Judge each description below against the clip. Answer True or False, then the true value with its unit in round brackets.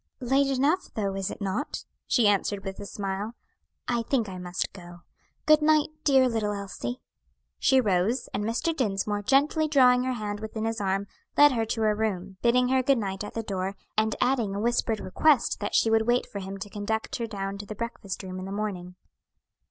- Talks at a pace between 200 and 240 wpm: True (205 wpm)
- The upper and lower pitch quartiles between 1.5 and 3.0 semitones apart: False (4.1 semitones)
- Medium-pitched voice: False (215 Hz)